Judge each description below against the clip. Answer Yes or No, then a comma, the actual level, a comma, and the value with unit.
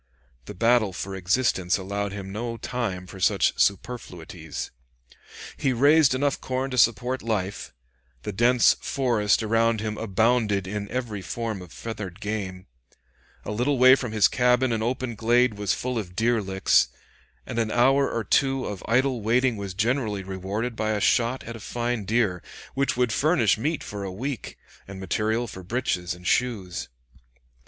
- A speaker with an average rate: Yes, average, 165 wpm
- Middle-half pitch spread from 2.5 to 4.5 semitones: Yes, average, 3.9 semitones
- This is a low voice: Yes, low, 110 Hz